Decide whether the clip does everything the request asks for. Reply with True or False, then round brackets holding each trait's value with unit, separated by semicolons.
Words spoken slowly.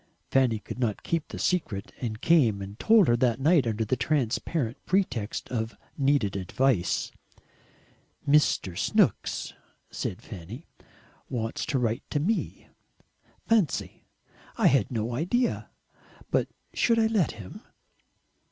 True (125 wpm)